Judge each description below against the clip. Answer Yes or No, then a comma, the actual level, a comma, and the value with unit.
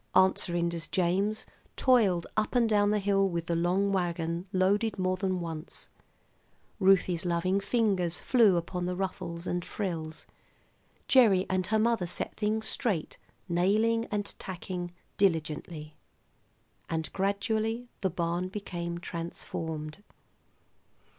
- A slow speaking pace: Yes, slow, 120 wpm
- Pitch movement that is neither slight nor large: Yes, average, 3.2 semitones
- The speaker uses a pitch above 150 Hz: Yes, medium, 185 Hz